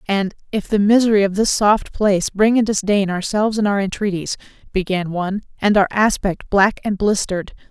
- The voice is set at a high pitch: Yes, high, 200 Hz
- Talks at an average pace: Yes, average, 180 wpm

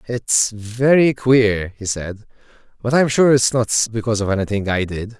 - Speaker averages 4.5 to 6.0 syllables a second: Yes, 4.6 syllables/s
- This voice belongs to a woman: No, male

